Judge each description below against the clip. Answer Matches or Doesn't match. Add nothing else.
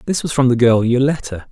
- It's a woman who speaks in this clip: Doesn't match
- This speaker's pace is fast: Matches